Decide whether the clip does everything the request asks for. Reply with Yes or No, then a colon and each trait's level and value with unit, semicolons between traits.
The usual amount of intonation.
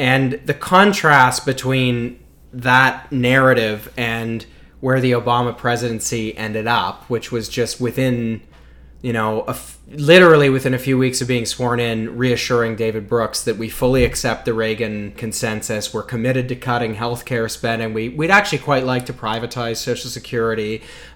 No: narrow, 2.3 semitones